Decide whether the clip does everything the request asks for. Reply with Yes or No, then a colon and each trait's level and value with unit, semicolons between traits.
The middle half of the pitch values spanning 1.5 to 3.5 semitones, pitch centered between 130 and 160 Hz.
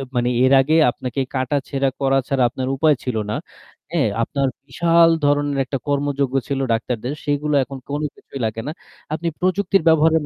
Yes: narrow, 2.5 semitones; medium, 140 Hz